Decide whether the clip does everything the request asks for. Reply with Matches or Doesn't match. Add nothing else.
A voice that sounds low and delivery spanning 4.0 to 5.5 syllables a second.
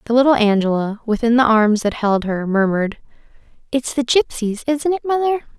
Doesn't match